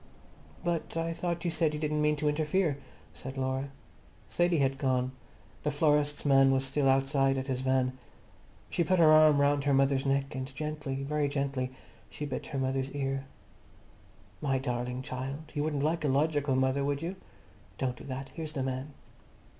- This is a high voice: No, medium, 140 Hz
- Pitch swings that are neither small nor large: No, narrow, 2.2 semitones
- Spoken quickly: No, average, 180 wpm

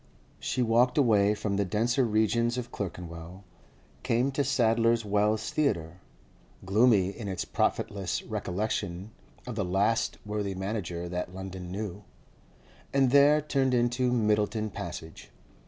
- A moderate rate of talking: No, slow, 125 wpm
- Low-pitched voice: Yes, low, 105 Hz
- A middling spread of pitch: Yes, average, 4.1 semitones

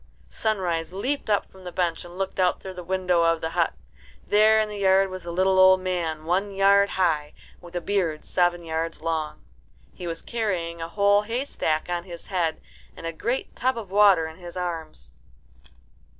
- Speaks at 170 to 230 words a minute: Yes, average, 190 wpm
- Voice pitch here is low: No, medium, 180 Hz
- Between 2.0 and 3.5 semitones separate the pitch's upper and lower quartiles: Yes, average, 3.0 semitones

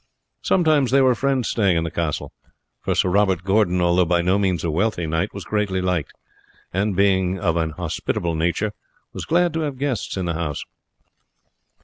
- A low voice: Yes, very low, 95 Hz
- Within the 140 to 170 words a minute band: No, average, 180 wpm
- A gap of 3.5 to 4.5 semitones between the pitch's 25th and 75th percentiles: Yes, average, 4.2 semitones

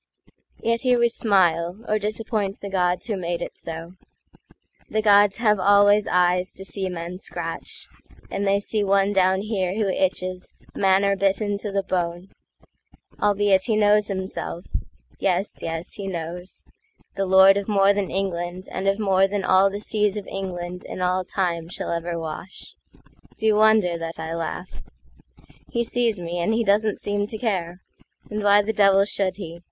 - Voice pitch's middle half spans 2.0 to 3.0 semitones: Yes, narrow, 2.4 semitones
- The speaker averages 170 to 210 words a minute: No, average, 145 wpm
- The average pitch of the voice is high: Yes, high, 195 Hz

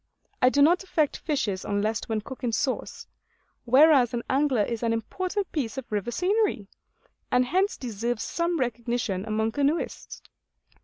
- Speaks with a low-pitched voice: No, very high, 250 Hz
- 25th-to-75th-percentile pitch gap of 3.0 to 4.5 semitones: No, average, 5.3 semitones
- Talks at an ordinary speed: Yes, average, 150 wpm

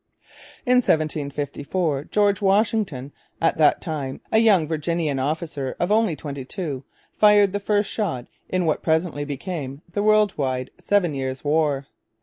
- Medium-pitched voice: Yes, medium, 160 Hz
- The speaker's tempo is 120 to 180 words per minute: Yes, average, 140 wpm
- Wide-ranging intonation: Yes, wide, 6.0 semitones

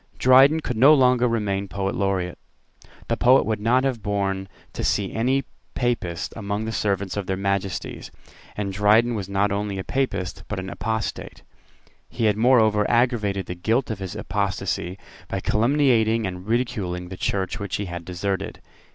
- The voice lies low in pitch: Yes, low, 105 Hz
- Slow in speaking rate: No, average, 165 wpm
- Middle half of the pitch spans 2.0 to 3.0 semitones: No, average, 3.4 semitones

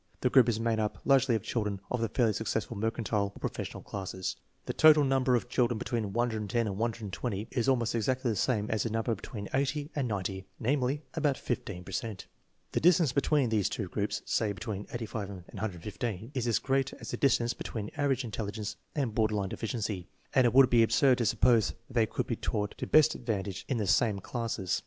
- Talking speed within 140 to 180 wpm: No, fast, 205 wpm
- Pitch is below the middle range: Yes, low, 115 Hz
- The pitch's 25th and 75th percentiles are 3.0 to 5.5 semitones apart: Yes, average, 3.5 semitones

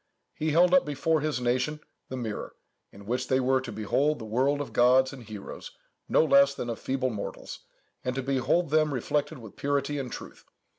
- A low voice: Yes, low, 130 Hz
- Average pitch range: Yes, average, 3.0 semitones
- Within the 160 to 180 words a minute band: No, average, 195 wpm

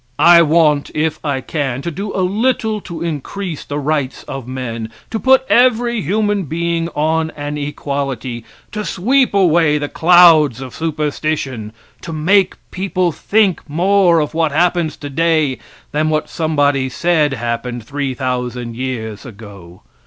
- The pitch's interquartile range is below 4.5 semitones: No, average, 4.8 semitones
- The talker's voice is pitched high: No, medium, 155 Hz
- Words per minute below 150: Yes, average, 140 wpm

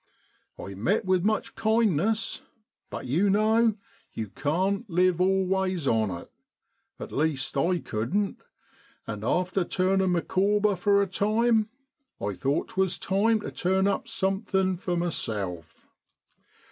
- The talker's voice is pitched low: No, high, 190 Hz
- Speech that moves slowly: Yes, slow, 125 wpm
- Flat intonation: No, average, 4.4 semitones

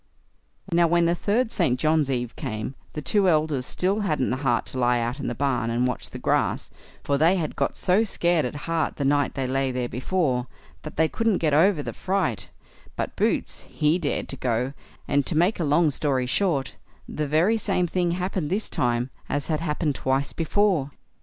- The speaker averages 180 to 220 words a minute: Yes, average, 200 wpm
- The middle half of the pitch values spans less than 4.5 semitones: No, average, 4.9 semitones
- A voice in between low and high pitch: Yes, medium, 150 Hz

